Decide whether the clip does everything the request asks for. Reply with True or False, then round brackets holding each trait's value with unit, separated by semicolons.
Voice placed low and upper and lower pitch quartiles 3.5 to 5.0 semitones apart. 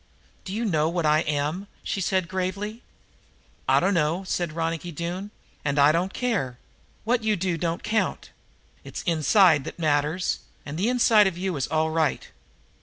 False (175 Hz; 3.9 semitones)